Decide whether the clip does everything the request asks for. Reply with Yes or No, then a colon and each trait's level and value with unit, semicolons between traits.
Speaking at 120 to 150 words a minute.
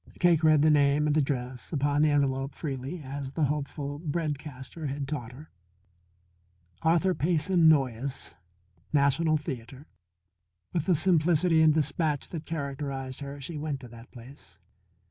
Yes: average, 145 wpm